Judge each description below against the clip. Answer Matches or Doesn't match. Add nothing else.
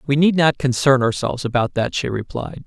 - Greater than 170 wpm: Matches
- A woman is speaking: Doesn't match